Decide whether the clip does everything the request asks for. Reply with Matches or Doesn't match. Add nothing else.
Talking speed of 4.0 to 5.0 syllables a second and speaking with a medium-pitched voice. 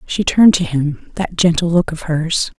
Matches